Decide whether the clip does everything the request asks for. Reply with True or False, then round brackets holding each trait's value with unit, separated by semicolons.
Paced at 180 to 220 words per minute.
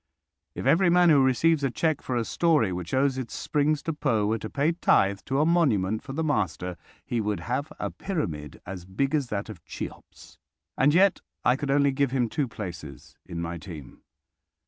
True (200 wpm)